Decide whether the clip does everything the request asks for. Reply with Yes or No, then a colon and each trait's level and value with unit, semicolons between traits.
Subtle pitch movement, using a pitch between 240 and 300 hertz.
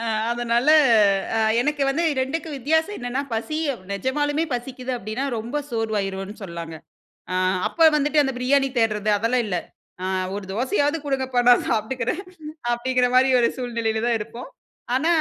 No: average, 3.8 semitones; very high, 250 Hz